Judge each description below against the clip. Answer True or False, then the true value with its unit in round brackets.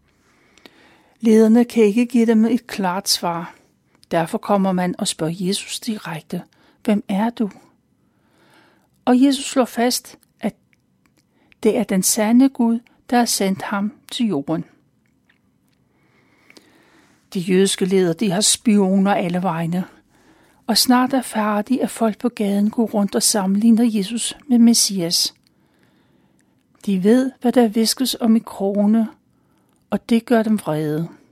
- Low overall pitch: False (220 Hz)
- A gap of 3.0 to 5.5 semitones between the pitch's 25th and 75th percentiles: True (3.5 semitones)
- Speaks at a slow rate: True (135 wpm)